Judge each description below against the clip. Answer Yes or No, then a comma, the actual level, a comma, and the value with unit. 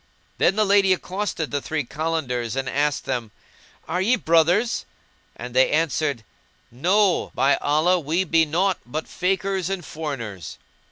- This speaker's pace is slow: No, average, 145 wpm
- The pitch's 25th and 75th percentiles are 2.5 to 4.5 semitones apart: No, average, 4.9 semitones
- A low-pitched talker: No, medium, 165 Hz